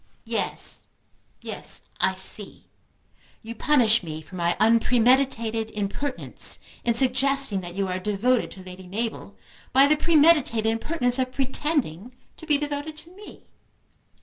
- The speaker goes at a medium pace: No, slow, 130 wpm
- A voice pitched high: Yes, high, 245 Hz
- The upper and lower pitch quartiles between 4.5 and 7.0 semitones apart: Yes, average, 5.2 semitones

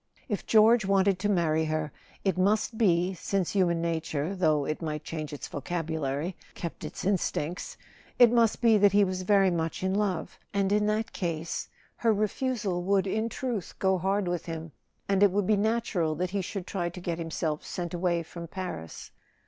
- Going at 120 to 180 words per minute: No, average, 190 wpm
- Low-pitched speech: No, medium, 185 Hz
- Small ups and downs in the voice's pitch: No, average, 3.6 semitones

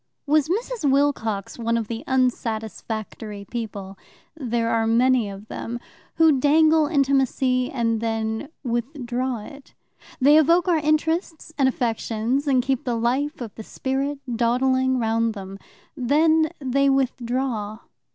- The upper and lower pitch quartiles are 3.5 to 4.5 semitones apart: Yes, average, 3.8 semitones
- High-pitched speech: Yes, very high, 255 Hz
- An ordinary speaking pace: No, slow, 130 wpm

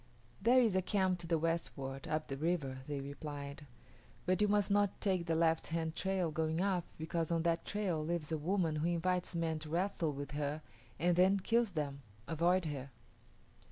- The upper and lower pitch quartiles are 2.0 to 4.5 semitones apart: Yes, average, 3.2 semitones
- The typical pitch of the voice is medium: Yes, medium, 165 Hz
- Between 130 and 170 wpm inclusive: No, average, 190 wpm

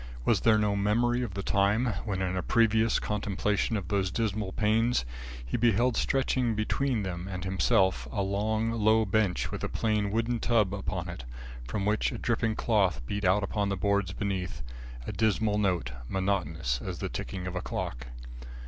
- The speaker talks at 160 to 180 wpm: Yes, average, 175 wpm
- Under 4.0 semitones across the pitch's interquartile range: Yes, average, 2.9 semitones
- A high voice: No, low, 100 Hz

